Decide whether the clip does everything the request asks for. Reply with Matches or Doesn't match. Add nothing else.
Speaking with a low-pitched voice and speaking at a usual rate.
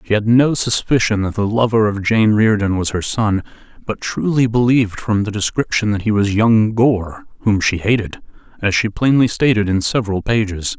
Matches